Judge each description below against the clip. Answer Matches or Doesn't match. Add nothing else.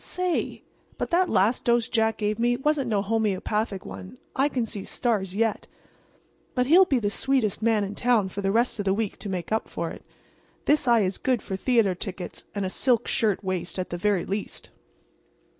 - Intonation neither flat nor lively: Matches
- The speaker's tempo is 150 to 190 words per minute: Doesn't match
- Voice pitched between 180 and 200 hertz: Doesn't match